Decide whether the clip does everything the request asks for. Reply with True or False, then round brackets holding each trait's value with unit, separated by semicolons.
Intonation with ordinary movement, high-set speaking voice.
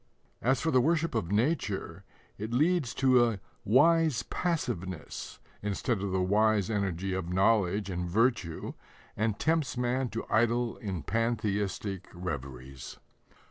False (4.7 semitones; 110 Hz)